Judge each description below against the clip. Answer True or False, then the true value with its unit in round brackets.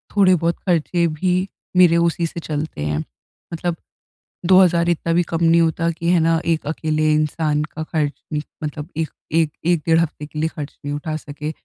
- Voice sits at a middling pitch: True (160 Hz)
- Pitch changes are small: True (1.8 semitones)